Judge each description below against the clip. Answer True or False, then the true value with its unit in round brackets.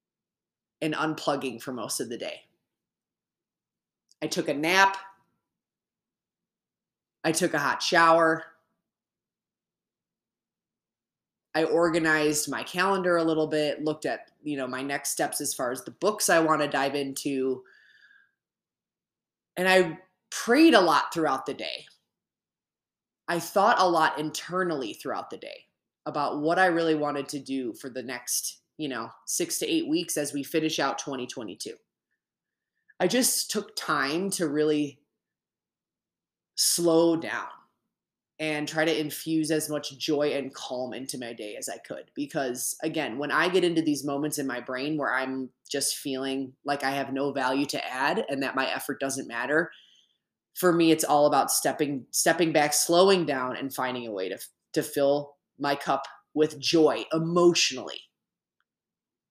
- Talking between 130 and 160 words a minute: True (150 wpm)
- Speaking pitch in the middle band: True (150 Hz)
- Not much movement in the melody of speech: False (3.5 semitones)